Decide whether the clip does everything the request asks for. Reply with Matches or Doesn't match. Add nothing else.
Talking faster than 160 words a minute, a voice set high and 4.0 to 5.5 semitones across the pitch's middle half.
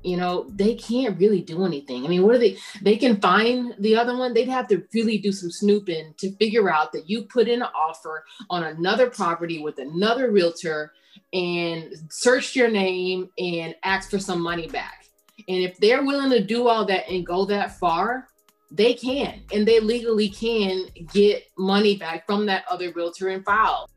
Matches